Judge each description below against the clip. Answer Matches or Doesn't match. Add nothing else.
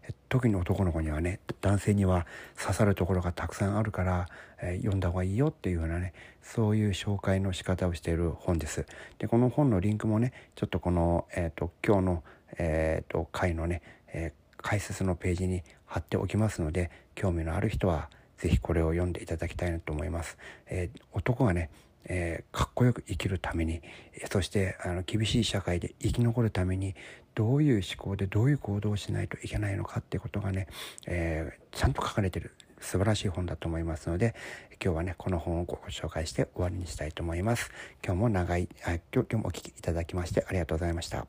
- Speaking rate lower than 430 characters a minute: Matches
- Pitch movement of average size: Matches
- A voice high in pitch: Doesn't match